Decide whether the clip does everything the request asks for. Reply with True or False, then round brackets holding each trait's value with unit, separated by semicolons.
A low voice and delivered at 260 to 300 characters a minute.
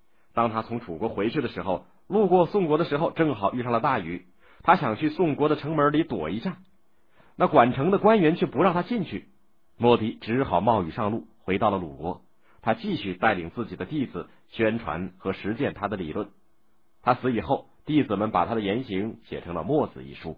True (120 Hz; 290 characters per minute)